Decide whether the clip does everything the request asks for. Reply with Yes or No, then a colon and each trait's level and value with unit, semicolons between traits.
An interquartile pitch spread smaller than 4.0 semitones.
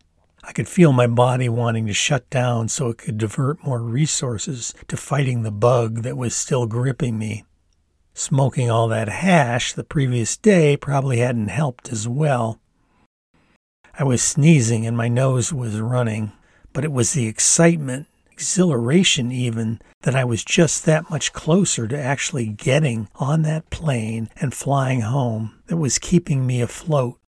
No: average, 4.3 semitones